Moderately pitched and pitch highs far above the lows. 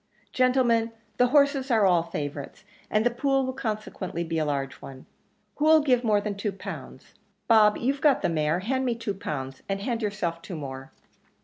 No: high, 210 Hz; wide, 7.2 semitones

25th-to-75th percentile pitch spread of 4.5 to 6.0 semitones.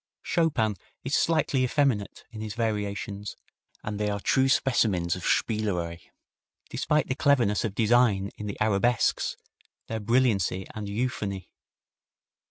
No: average, 3.8 semitones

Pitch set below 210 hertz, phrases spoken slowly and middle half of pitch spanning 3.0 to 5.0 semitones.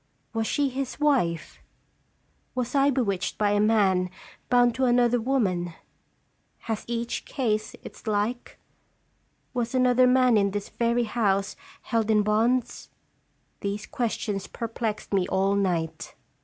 No: high, 225 Hz; slow, 130 wpm; average, 3.6 semitones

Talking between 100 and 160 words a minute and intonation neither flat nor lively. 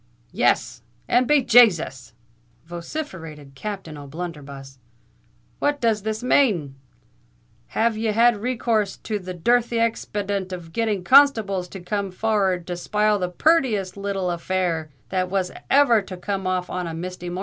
Yes: average, 145 wpm; average, 4.1 semitones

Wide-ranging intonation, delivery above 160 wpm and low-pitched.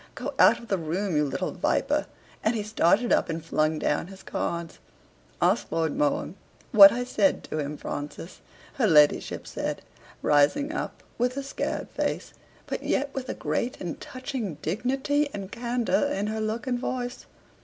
No: wide, 7.3 semitones; average, 170 wpm; high, 210 Hz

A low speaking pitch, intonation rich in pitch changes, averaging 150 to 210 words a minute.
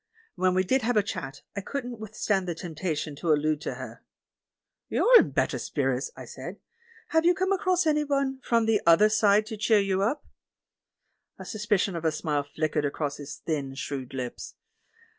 No: high, 195 Hz; wide, 7.5 semitones; average, 180 wpm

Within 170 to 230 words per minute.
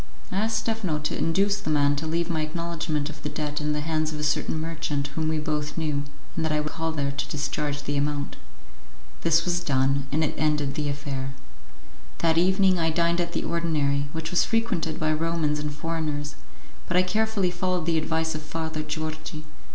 Yes: average, 200 wpm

